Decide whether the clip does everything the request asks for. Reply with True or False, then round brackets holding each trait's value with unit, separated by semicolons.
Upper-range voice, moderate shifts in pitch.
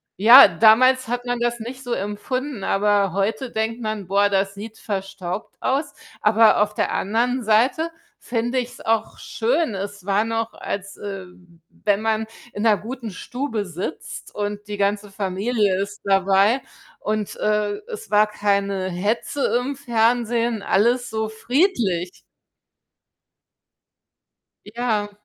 True (215 Hz; 3.2 semitones)